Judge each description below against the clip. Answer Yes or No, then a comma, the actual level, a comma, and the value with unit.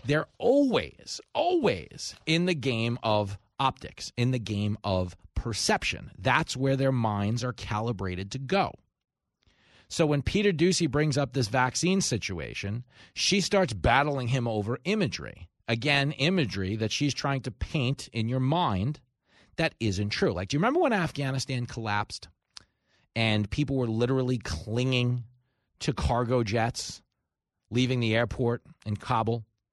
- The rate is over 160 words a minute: No, average, 140 wpm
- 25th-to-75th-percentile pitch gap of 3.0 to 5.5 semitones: Yes, average, 4.9 semitones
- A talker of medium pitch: No, low, 125 Hz